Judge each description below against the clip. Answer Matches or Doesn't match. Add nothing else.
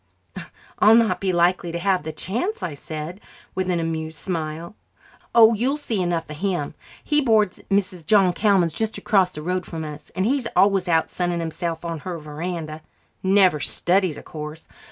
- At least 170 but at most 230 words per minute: Matches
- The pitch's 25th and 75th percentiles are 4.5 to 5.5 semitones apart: Doesn't match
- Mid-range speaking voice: Matches